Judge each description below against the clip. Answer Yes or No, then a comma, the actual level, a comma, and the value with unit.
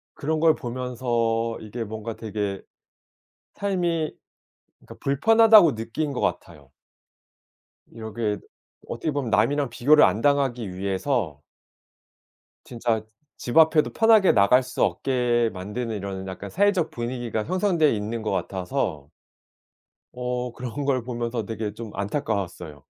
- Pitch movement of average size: Yes, average, 5.0 semitones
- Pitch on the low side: Yes, low, 120 Hz